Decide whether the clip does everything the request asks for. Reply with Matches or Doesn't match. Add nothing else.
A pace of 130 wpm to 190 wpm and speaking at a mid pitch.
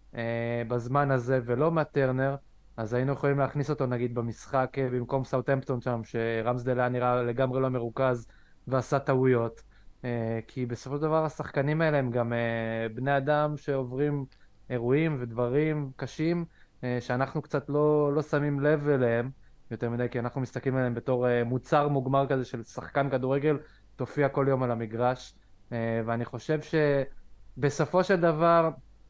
Doesn't match